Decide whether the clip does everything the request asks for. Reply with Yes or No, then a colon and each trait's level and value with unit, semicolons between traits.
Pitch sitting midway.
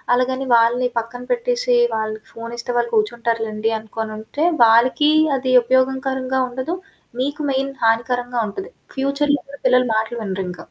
No: high, 245 Hz